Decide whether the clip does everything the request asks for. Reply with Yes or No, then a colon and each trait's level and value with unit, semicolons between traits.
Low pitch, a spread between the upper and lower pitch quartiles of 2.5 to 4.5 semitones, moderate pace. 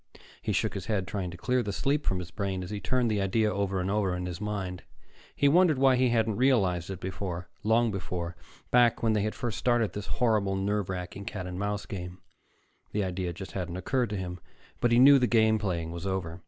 No: low, 100 Hz; average, 3.9 semitones; fast, 225 wpm